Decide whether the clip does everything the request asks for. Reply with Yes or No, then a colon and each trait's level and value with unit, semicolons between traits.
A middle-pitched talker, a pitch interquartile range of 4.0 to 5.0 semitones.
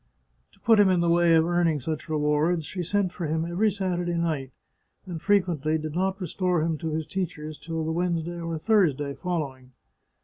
No: medium, 170 Hz; narrow, 2.5 semitones